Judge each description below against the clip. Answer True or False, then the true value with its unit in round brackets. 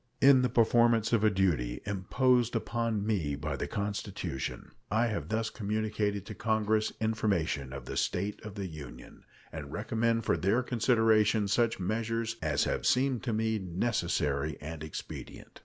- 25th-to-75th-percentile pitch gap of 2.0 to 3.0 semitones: False (3.8 semitones)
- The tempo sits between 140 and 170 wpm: True (155 wpm)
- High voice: False (110 Hz)